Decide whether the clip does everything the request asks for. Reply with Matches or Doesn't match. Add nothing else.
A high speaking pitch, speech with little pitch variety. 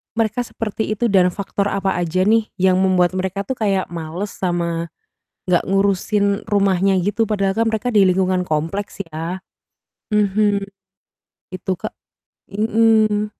Matches